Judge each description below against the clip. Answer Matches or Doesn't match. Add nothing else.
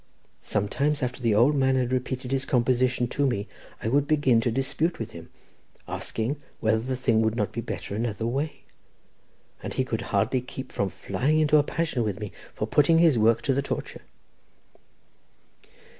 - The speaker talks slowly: Doesn't match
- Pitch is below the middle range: Matches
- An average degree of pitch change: Matches